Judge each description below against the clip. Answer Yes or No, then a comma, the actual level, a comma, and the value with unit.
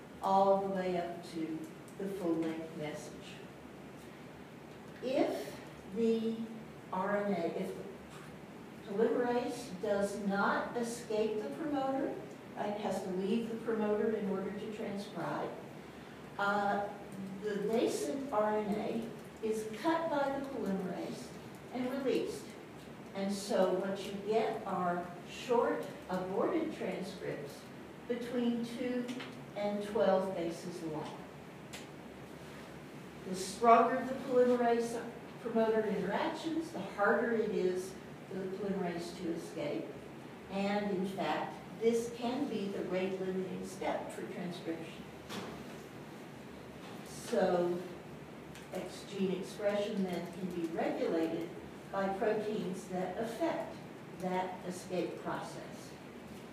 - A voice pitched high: Yes, high, 205 Hz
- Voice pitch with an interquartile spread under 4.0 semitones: Yes, average, 3.3 semitones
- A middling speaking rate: No, slow, 100 wpm